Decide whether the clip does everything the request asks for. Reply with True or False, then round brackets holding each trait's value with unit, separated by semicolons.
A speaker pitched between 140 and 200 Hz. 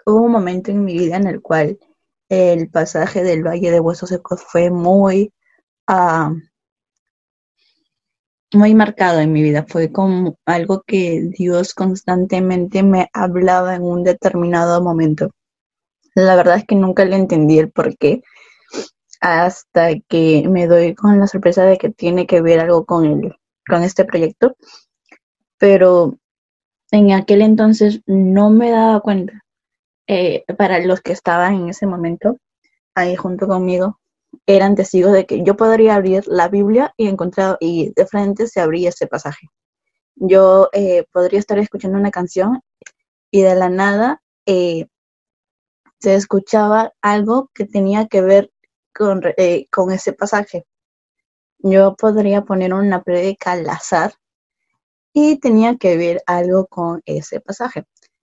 True (190 Hz)